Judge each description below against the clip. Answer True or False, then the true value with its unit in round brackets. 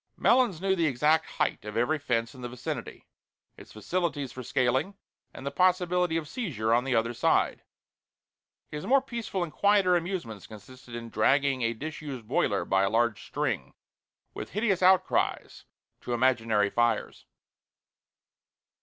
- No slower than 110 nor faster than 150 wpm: True (145 wpm)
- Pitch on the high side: False (140 Hz)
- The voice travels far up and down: True (7.3 semitones)